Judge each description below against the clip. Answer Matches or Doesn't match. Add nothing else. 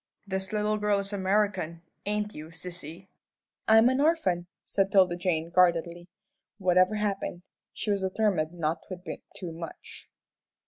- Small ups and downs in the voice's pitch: Doesn't match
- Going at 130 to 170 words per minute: Matches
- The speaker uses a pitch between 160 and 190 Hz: Matches